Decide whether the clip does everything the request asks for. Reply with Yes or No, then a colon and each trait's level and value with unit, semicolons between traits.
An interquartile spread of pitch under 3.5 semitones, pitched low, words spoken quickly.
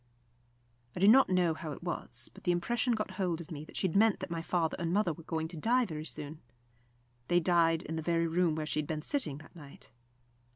No: narrow, 2.6 semitones; medium, 170 Hz; fast, 240 wpm